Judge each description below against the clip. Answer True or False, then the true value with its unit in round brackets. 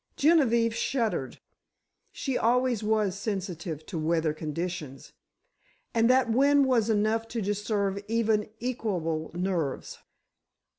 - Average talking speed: False (100 wpm)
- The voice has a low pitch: False (210 Hz)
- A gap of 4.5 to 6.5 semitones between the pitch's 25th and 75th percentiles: True (4.8 semitones)